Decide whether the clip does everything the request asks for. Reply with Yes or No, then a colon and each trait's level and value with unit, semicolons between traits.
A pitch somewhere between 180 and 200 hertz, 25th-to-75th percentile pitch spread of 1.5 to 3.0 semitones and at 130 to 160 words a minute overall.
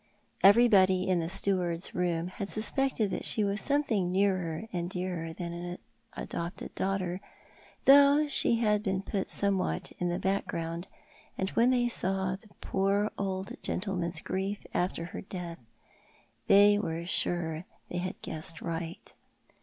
Yes: high, 190 Hz; average, 2.7 semitones; average, 145 wpm